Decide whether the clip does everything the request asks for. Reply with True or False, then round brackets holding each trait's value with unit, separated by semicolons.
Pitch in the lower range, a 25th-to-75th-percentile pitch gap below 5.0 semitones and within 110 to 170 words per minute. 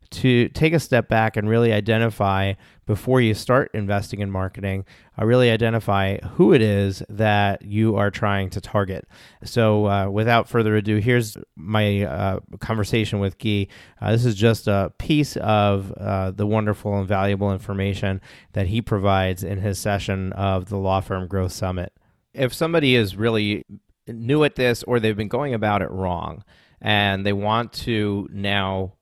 True (105 Hz; 2.5 semitones; 165 wpm)